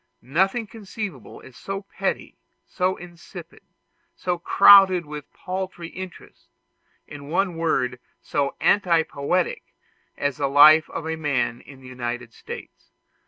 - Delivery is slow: Yes, slow, 125 wpm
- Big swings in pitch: No, average, 4.9 semitones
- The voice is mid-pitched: Yes, medium, 165 Hz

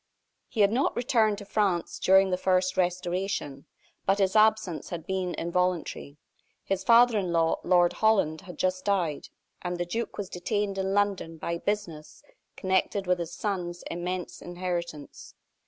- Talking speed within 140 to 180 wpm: Yes, average, 155 wpm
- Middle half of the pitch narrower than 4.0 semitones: Yes, narrow, 2.6 semitones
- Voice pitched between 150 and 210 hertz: Yes, medium, 185 Hz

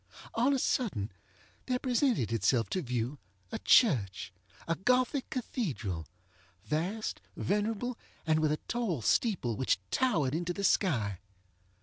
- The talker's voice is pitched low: No, medium, 160 Hz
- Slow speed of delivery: Yes, slow, 115 wpm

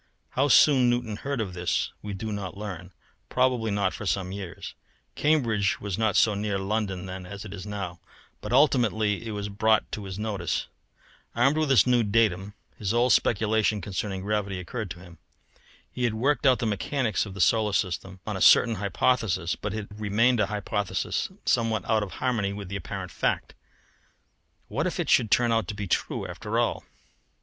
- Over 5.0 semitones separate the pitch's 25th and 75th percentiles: No, average, 2.8 semitones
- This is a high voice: No, low, 105 Hz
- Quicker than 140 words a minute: Yes, average, 185 wpm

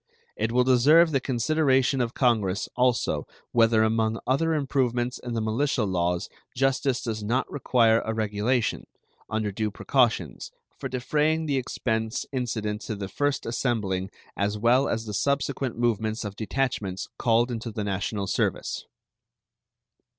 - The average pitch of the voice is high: No, low, 115 Hz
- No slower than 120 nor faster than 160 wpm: Yes, average, 140 wpm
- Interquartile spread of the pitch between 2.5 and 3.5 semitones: Yes, average, 3.2 semitones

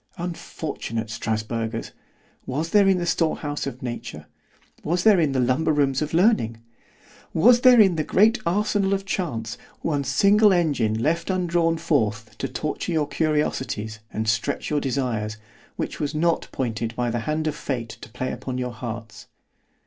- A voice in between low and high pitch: Yes, medium, 145 Hz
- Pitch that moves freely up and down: Yes, wide, 6.8 semitones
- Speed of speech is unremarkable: Yes, average, 160 wpm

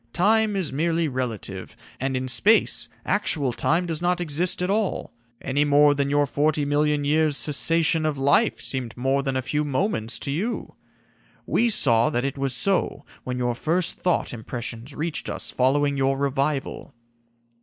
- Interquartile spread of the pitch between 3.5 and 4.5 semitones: Yes, average, 3.9 semitones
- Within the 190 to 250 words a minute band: No, average, 165 wpm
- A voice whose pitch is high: No, medium, 145 Hz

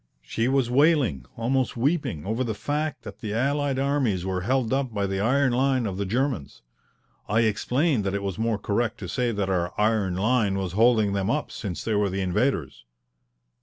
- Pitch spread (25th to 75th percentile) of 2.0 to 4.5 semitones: No, average, 5.1 semitones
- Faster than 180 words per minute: Yes, average, 195 wpm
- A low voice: Yes, low, 115 Hz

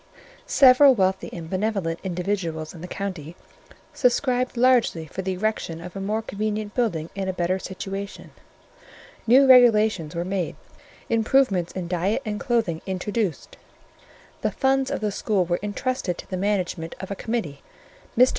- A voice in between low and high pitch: No, high, 195 Hz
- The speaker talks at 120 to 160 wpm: Yes, average, 150 wpm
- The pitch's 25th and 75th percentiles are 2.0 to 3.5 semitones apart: No, average, 4.1 semitones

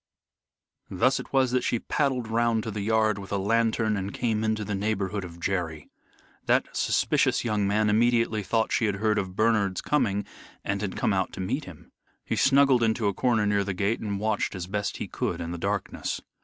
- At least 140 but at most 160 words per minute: No, fast, 205 wpm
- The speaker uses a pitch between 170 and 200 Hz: No, low, 105 Hz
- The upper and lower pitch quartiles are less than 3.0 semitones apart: Yes, narrow, 2.6 semitones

